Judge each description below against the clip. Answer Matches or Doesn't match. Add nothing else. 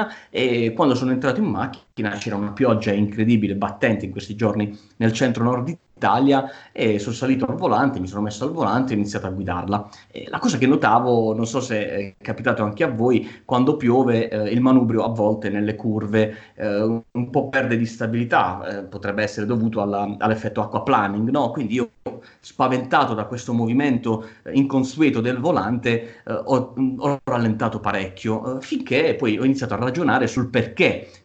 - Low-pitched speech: Matches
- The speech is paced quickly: Matches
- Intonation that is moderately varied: Matches